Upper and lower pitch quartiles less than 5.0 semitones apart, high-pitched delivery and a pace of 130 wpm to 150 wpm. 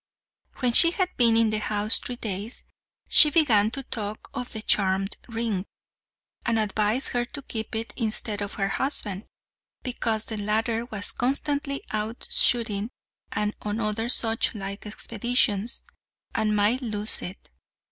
Yes: narrow, 2.6 semitones; high, 220 Hz; average, 145 wpm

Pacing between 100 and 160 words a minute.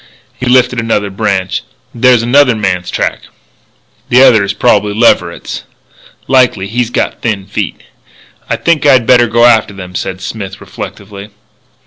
Yes: average, 140 wpm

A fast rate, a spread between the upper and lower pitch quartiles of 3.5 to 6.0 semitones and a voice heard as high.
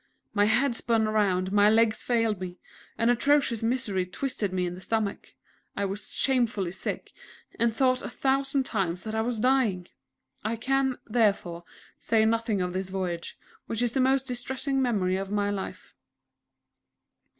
No: average, 160 wpm; average, 4.3 semitones; high, 220 Hz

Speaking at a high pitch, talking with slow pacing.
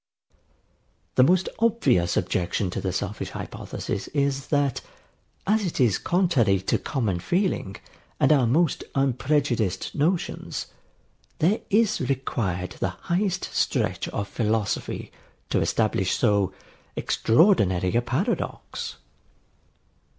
No: low, 130 Hz; slow, 110 wpm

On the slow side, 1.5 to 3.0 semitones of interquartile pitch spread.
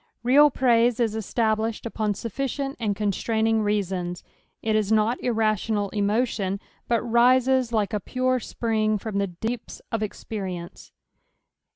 Yes: slow, 130 wpm; narrow, 2.5 semitones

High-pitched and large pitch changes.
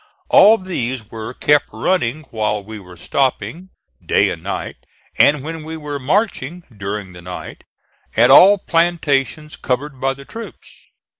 No: medium, 140 Hz; wide, 6.9 semitones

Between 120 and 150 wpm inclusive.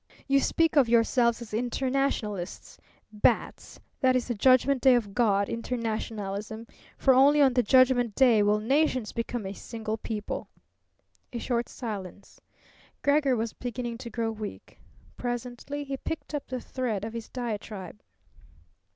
Yes: average, 140 wpm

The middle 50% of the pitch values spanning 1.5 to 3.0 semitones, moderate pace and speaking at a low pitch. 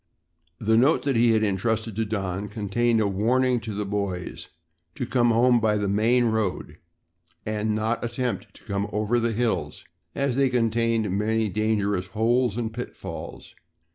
Yes: narrow, 2.4 semitones; average, 160 wpm; low, 110 Hz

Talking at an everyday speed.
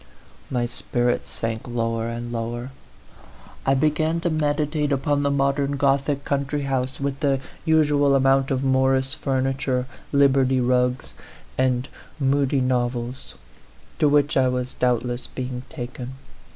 No: slow, 130 wpm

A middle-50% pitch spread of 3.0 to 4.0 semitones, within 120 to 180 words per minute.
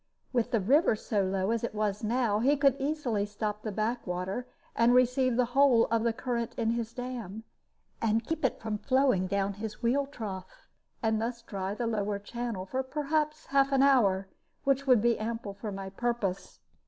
No: average, 3.6 semitones; average, 190 wpm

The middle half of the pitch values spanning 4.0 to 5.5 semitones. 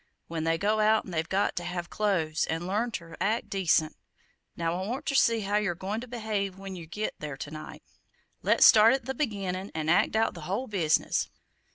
Yes: average, 4.3 semitones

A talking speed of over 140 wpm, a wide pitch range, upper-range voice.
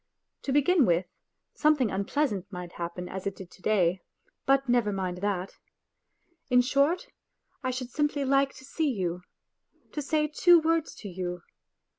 Yes: average, 155 wpm; wide, 7.6 semitones; high, 245 Hz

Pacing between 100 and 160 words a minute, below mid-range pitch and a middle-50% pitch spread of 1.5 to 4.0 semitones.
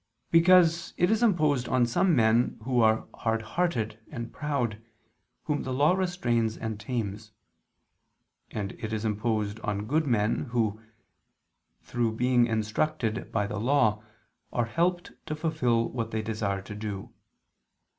No: average, 140 wpm; low, 115 Hz; average, 5.3 semitones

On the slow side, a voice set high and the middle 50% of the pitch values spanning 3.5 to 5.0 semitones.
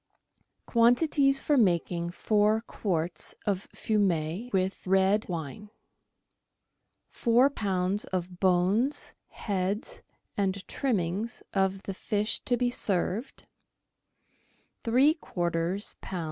Yes: slow, 100 wpm; high, 200 Hz; average, 4.1 semitones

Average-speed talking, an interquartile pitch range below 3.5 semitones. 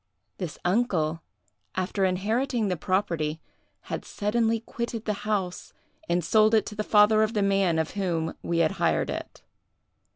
No: average, 155 wpm; average, 3.8 semitones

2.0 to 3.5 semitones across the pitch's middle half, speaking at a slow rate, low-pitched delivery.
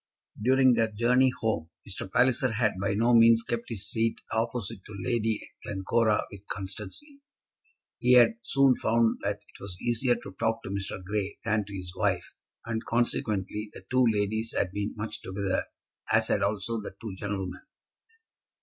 No: average, 2.8 semitones; average, 165 wpm; low, 110 Hz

